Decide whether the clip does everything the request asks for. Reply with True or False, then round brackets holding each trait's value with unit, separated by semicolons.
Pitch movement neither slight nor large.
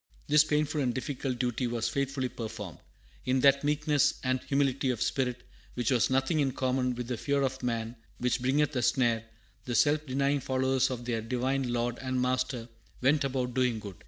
False (2.0 semitones)